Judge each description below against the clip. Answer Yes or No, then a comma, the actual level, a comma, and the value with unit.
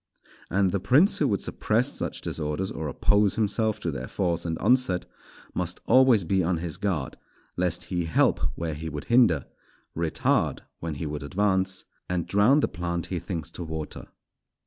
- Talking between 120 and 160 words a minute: No, average, 170 wpm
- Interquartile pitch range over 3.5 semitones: Yes, average, 4.0 semitones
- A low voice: Yes, very low, 90 Hz